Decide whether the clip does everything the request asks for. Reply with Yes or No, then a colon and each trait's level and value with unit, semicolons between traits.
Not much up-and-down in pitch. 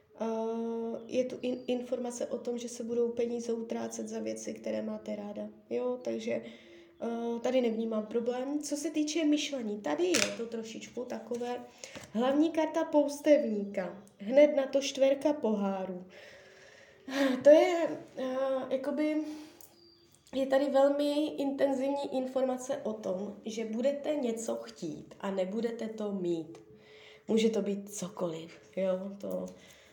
No: wide, 6.7 semitones